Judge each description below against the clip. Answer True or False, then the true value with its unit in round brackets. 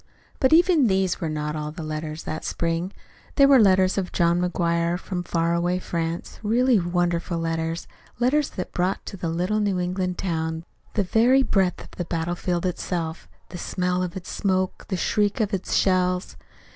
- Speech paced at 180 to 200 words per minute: True (185 wpm)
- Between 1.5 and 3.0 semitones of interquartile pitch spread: True (2.6 semitones)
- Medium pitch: True (180 Hz)